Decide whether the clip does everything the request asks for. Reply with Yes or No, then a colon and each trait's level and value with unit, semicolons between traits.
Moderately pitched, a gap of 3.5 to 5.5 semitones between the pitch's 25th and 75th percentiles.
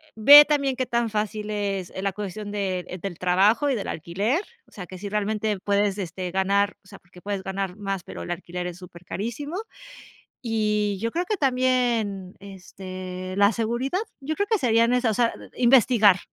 No: high, 205 Hz; average, 3.9 semitones